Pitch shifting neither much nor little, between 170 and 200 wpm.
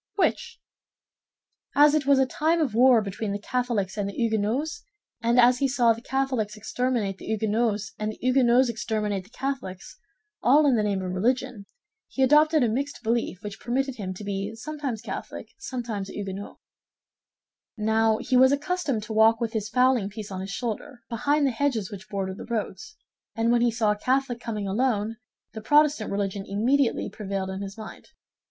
Yes: average, 4.1 semitones; average, 175 wpm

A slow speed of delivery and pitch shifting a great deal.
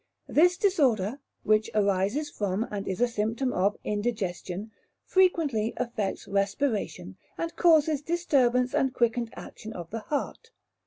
Yes: slow, 125 wpm; wide, 6.0 semitones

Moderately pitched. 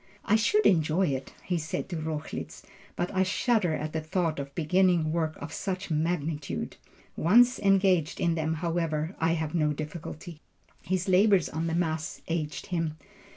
Yes: medium, 165 Hz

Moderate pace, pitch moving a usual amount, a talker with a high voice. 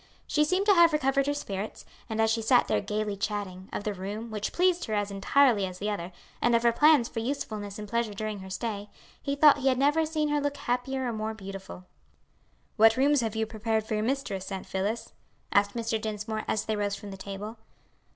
No: fast, 220 wpm; average, 4.6 semitones; high, 220 Hz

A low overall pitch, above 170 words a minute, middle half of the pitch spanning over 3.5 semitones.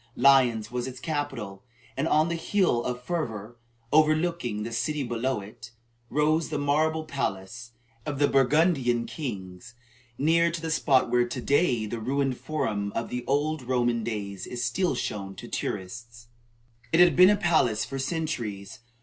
No: low, 130 Hz; average, 160 wpm; average, 5.1 semitones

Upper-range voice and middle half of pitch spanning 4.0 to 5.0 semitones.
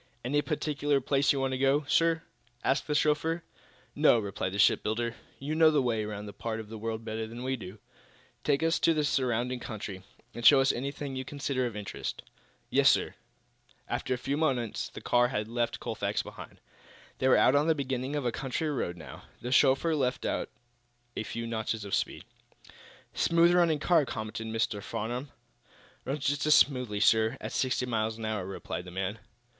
No: low, 125 Hz; average, 4.5 semitones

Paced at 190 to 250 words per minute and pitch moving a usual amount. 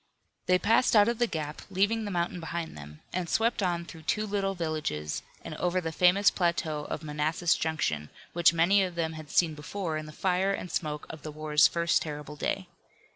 Yes: average, 200 wpm; average, 3.5 semitones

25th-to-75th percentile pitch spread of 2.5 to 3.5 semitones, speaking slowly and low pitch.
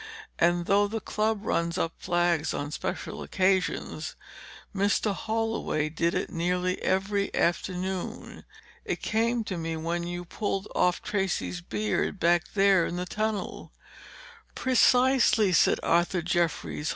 No: average, 3.1 semitones; slow, 125 wpm; medium, 185 Hz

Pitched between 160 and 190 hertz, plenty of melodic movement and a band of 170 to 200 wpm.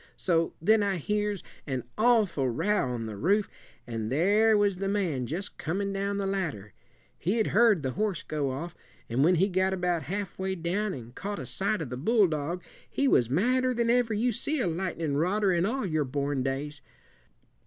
Yes: medium, 185 Hz; wide, 5.9 semitones; average, 190 wpm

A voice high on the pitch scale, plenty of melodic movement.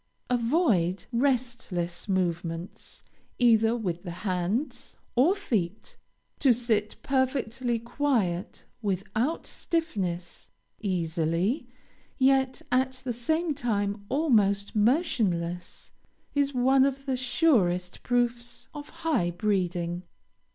Yes: high, 230 Hz; wide, 6.4 semitones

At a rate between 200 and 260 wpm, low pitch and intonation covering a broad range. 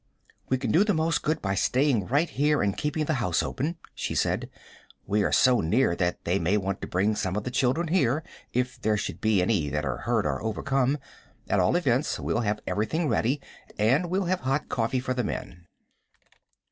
Yes: fast, 205 wpm; low, 125 Hz; wide, 6.3 semitones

